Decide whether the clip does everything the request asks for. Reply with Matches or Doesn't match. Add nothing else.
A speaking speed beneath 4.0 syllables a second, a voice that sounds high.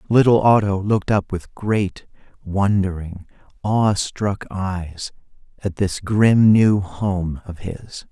Doesn't match